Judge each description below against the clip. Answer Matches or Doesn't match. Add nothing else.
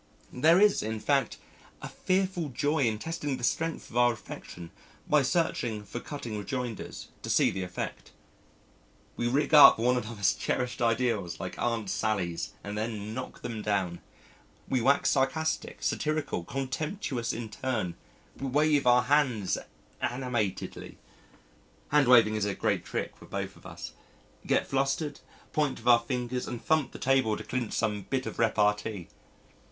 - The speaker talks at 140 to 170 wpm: Matches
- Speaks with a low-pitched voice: Matches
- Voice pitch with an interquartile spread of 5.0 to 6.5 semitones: Doesn't match